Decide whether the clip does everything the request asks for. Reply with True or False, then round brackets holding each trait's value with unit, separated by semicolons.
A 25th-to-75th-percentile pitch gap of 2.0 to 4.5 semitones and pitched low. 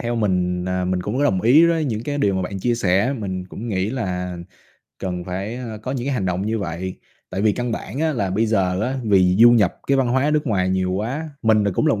False (4.9 semitones; 105 Hz)